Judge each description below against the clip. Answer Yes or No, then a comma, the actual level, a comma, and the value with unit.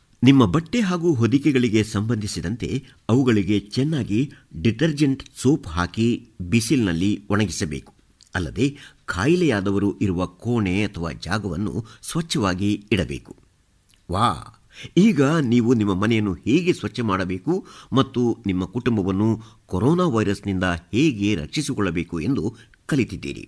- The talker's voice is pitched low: Yes, low, 110 Hz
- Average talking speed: Yes, average, 95 wpm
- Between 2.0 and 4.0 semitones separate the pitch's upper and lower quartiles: No, average, 5.1 semitones